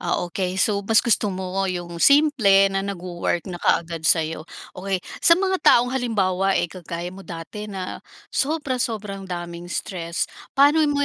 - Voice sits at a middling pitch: No, high, 195 Hz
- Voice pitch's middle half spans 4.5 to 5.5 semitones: Yes, average, 5.2 semitones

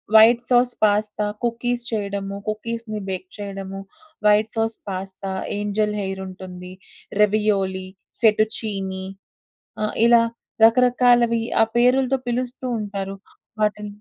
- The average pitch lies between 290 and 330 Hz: No, high, 210 Hz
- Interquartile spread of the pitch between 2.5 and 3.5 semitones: Yes, average, 3.1 semitones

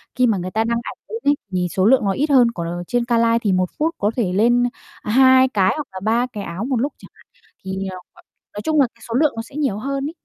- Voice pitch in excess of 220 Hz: Yes, high, 230 Hz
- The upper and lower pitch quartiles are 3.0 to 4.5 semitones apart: No, average, 5.2 semitones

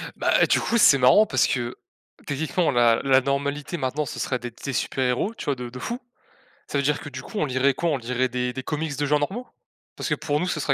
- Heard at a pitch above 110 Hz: Yes, medium, 140 Hz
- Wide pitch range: No, average, 2.9 semitones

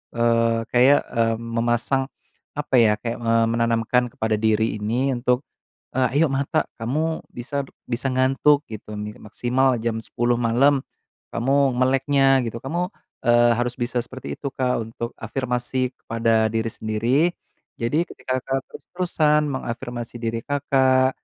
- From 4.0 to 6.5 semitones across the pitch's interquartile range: No, narrow, 2.6 semitones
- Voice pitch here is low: Yes, low, 120 Hz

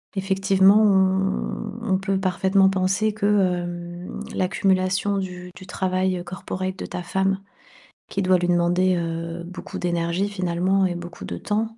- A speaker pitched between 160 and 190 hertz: Yes, medium, 185 Hz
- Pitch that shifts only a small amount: Yes, narrow, 1.5 semitones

